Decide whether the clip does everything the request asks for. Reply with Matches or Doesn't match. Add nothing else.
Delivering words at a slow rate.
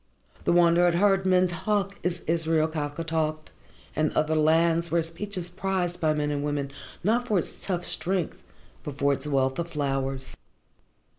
Doesn't match